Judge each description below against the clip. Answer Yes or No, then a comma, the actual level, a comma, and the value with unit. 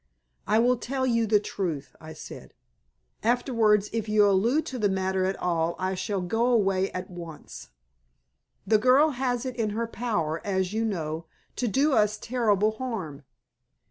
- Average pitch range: Yes, average, 4.2 semitones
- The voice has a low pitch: No, high, 210 Hz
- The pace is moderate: Yes, average, 165 wpm